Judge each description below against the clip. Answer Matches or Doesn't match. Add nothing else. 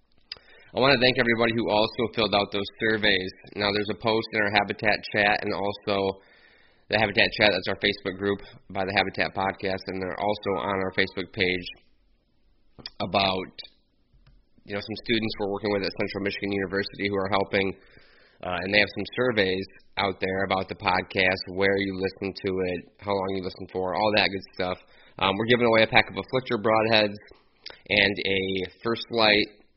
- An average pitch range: Doesn't match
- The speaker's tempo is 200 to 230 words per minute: Doesn't match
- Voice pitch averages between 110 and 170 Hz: Doesn't match